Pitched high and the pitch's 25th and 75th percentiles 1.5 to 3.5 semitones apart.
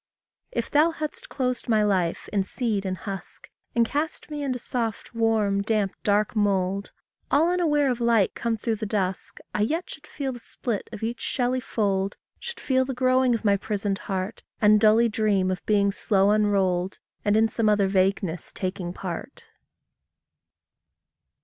No: high, 215 Hz; average, 3.9 semitones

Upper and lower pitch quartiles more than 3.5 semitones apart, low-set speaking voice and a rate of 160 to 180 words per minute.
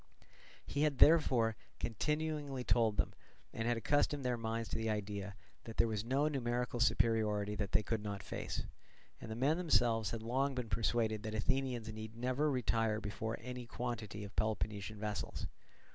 No: average, 2.8 semitones; low, 115 Hz; average, 165 wpm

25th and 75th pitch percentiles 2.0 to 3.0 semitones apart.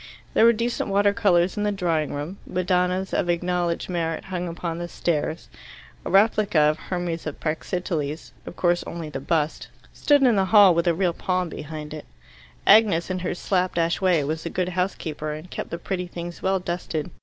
Yes: narrow, 2.5 semitones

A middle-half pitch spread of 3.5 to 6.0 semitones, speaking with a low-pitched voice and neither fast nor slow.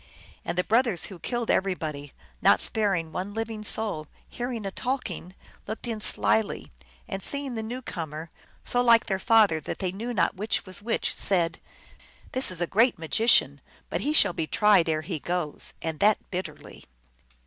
No: average, 4.9 semitones; high, 200 Hz; average, 180 wpm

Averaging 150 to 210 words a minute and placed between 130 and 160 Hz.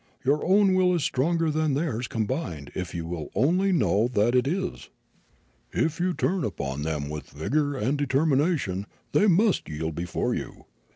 Yes: average, 170 wpm; low, 135 Hz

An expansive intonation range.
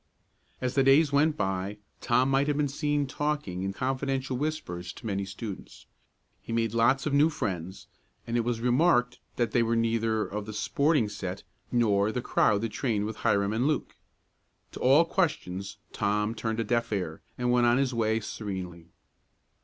No: average, 4.8 semitones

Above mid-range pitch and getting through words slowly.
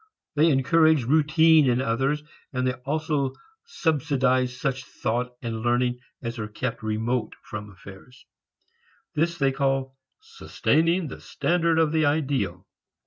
No: low, 135 Hz; slow, 130 wpm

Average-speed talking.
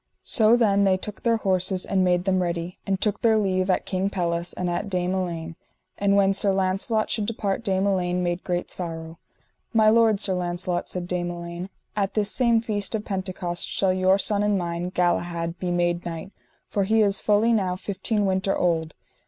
Yes: average, 195 wpm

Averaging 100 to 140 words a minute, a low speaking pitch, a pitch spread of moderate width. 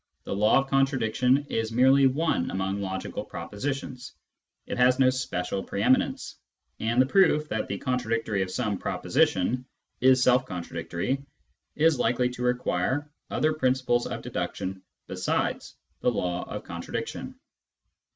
Yes: slow, 135 wpm; low, 125 Hz; average, 4.6 semitones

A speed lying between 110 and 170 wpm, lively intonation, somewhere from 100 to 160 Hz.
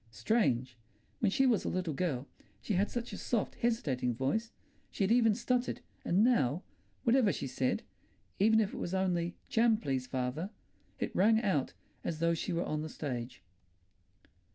No: average, 160 wpm; wide, 8.7 semitones; medium, 180 Hz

